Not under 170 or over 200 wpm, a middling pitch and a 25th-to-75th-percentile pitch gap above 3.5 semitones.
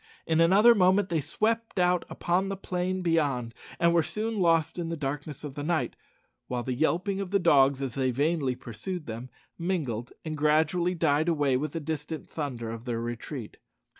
Yes: average, 180 wpm; medium, 160 Hz; average, 4.9 semitones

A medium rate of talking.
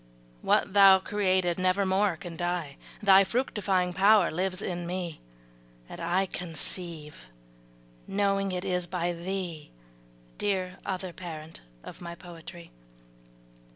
No: slow, 120 wpm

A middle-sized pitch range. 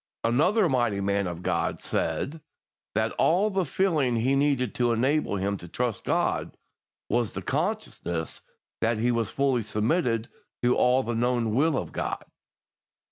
Yes: average, 4.1 semitones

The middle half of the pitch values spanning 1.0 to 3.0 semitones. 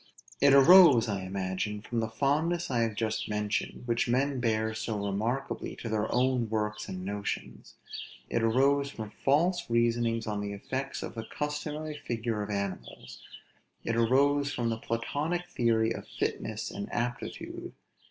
No: average, 4.1 semitones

